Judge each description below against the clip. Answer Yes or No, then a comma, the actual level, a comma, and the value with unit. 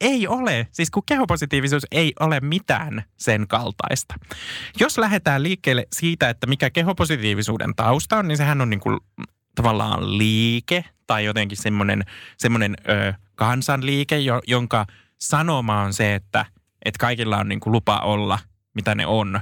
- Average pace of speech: Yes, average, 140 wpm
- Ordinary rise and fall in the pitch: No, wide, 6.2 semitones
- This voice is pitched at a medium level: No, low, 120 Hz